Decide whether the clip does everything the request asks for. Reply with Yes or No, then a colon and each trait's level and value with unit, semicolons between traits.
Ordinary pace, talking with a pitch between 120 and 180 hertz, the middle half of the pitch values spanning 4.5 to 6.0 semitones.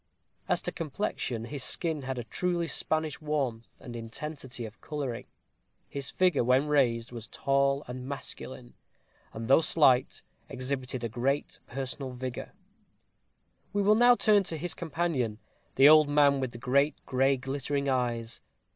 No: average, 145 wpm; low, 135 Hz; average, 3.5 semitones